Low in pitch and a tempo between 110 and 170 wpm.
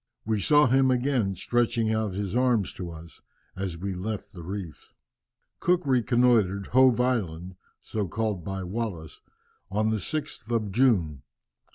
Yes: low, 110 Hz; average, 145 wpm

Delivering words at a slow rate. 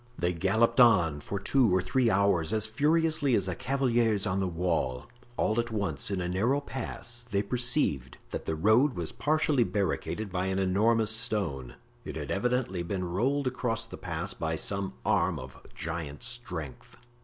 No: average, 170 wpm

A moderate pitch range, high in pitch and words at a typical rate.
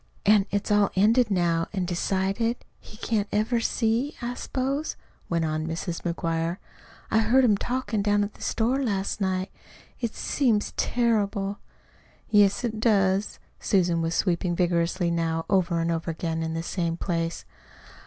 Yes: average, 4.6 semitones; high, 195 Hz; average, 155 wpm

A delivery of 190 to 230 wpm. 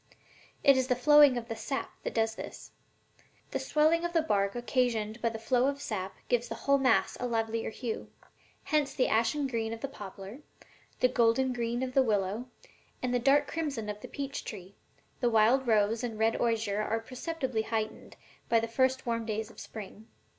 Yes: average, 195 wpm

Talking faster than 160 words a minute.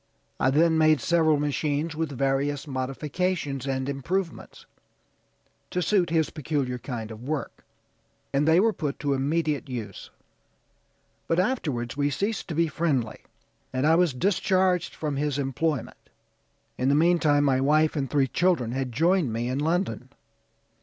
No: average, 145 wpm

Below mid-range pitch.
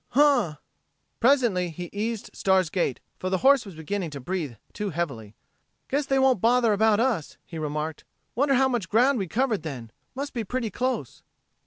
No: high, 205 Hz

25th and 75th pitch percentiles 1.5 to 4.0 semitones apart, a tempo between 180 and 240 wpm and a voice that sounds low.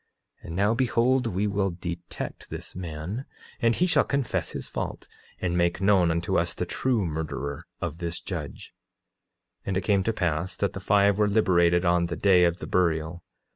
Yes: average, 3.1 semitones; average, 190 wpm; very low, 90 Hz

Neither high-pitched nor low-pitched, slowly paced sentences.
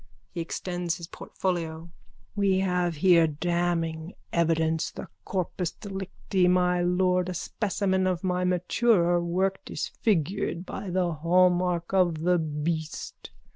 Yes: medium, 180 Hz; slow, 120 wpm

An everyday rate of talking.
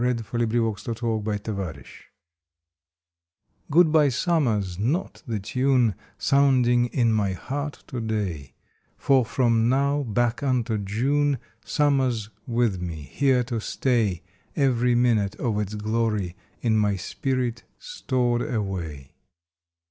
No: slow, 125 wpm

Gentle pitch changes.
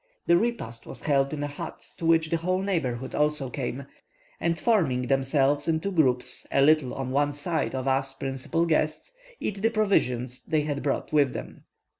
No: average, 3.7 semitones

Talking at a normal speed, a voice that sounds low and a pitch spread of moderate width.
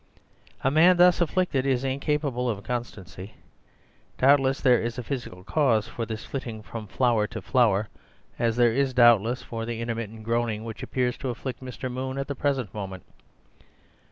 Yes: average, 165 wpm; low, 120 Hz; average, 3.0 semitones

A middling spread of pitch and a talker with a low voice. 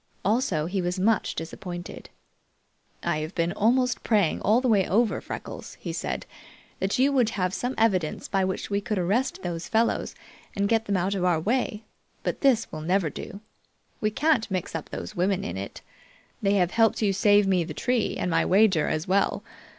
No: average, 3.9 semitones; high, 200 Hz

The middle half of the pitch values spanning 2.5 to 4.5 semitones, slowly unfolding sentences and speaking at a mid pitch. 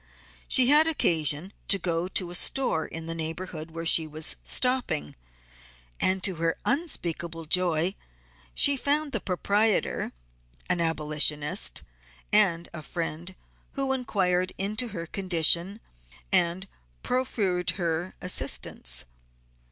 Yes: average, 4.0 semitones; slow, 115 wpm; medium, 175 Hz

